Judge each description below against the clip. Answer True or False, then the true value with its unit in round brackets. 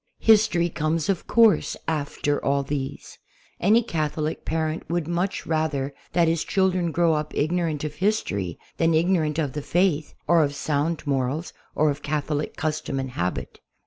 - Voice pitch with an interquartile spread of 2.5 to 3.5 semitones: True (2.9 semitones)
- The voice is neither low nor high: True (155 Hz)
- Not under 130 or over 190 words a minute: True (160 wpm)